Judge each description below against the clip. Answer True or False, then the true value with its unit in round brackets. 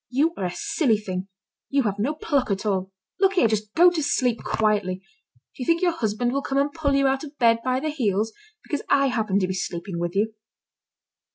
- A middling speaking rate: False (220 wpm)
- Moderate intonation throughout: False (5.9 semitones)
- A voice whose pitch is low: False (230 Hz)